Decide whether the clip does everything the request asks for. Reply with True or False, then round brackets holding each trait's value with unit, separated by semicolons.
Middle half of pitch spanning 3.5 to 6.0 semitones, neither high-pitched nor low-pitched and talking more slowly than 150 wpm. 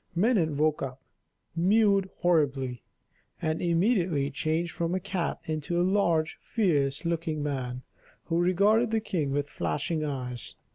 True (4.3 semitones; 165 Hz; 135 wpm)